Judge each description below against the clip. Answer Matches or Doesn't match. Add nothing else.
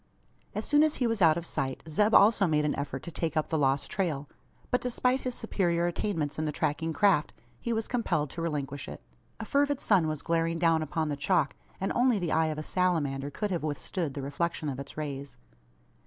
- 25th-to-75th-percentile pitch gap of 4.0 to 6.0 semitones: Matches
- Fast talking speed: Matches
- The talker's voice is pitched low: Doesn't match